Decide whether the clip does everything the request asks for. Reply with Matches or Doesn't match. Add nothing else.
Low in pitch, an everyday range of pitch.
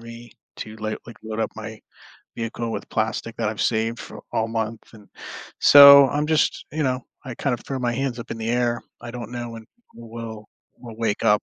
Doesn't match